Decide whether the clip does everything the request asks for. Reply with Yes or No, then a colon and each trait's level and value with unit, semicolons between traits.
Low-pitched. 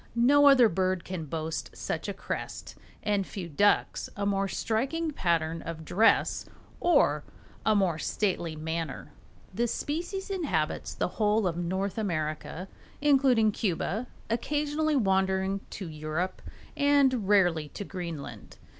No: high, 195 Hz